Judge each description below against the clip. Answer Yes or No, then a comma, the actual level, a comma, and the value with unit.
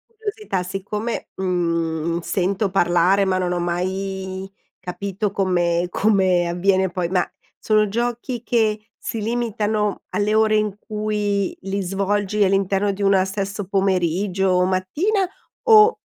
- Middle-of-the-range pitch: No, high, 195 Hz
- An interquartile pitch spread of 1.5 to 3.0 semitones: Yes, narrow, 2.4 semitones